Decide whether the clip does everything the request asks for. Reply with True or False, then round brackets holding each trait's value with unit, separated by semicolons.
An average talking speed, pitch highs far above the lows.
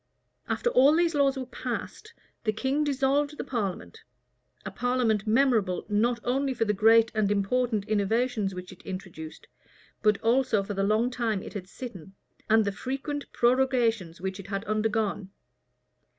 False (155 wpm; 4.3 semitones)